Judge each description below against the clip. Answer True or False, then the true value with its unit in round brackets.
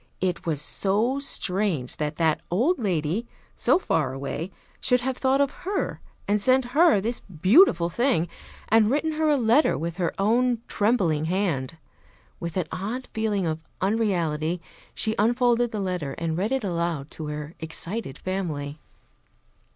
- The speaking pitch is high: True (195 Hz)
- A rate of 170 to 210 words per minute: False (150 wpm)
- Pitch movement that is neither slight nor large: False (6.7 semitones)